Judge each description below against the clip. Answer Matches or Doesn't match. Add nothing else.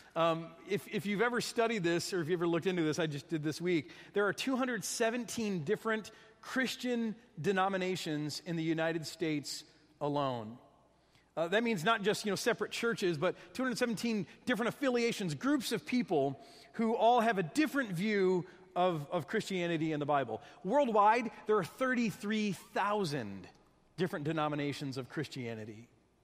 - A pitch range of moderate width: Doesn't match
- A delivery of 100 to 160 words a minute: Matches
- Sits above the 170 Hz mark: Matches